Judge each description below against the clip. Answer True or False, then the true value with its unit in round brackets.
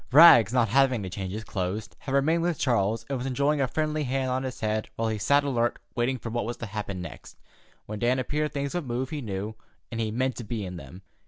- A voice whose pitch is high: False (120 Hz)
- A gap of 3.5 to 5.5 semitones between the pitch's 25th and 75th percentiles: True (4.1 semitones)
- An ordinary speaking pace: False (245 wpm)